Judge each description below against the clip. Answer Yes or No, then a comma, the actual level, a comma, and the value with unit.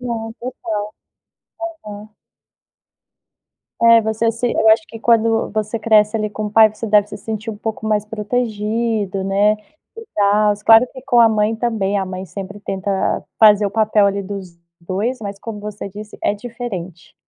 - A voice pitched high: Yes, high, 215 Hz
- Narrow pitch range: Yes, narrow, 1.9 semitones